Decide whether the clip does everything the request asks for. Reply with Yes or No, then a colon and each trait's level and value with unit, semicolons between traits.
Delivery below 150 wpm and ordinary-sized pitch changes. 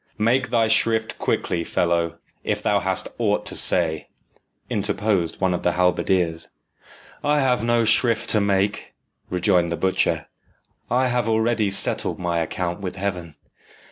Yes: average, 140 wpm; average, 4.4 semitones